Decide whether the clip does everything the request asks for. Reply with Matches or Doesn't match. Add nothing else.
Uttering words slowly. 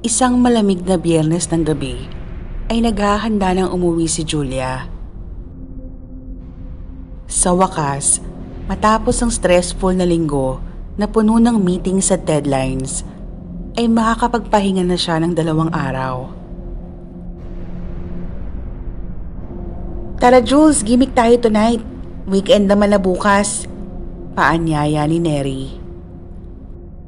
Matches